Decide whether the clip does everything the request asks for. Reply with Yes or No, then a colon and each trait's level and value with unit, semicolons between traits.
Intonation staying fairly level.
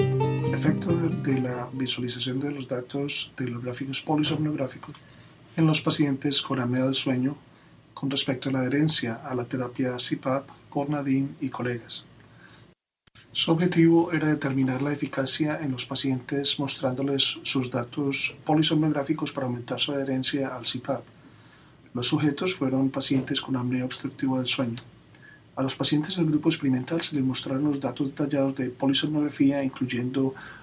Yes: narrow, 2.3 semitones